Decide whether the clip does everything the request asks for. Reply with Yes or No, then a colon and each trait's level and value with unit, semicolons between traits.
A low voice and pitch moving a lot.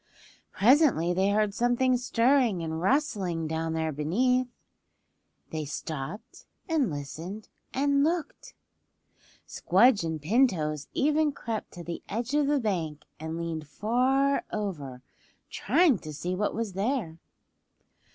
No: high, 205 Hz; wide, 8.0 semitones